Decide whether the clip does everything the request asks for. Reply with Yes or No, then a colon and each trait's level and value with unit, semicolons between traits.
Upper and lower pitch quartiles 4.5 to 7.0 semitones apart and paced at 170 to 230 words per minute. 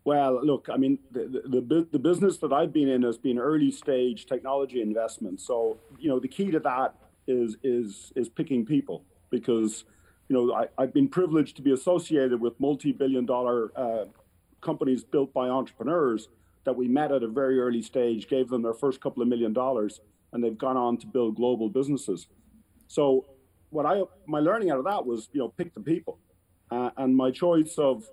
No: average, 3.4 semitones; average, 195 wpm